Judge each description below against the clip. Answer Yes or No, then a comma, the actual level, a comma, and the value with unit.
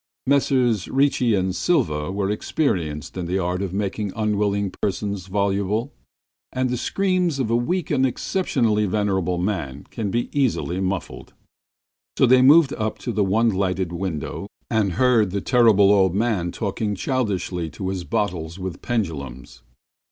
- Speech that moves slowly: No, average, 150 wpm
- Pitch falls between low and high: No, low, 100 Hz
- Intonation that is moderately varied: Yes, average, 4.5 semitones